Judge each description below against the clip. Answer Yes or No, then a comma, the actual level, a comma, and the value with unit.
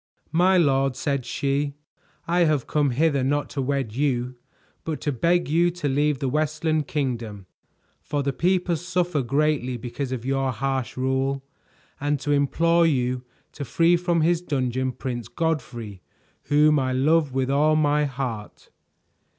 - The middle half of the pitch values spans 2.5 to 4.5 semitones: Yes, average, 3.1 semitones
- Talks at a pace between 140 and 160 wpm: Yes, average, 150 wpm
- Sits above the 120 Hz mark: Yes, medium, 140 Hz